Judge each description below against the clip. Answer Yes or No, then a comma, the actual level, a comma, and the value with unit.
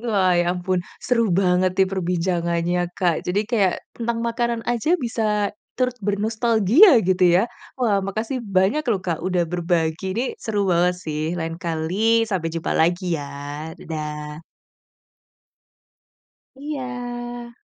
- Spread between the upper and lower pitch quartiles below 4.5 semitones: No, average, 5.2 semitones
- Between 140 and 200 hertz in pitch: Yes, high, 190 Hz